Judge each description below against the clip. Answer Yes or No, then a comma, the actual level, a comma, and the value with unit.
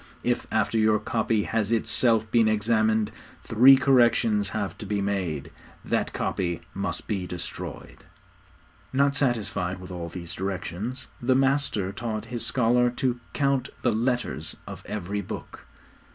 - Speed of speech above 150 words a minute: No, slow, 135 wpm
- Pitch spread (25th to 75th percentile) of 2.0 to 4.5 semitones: Yes, average, 3.7 semitones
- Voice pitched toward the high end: No, low, 110 Hz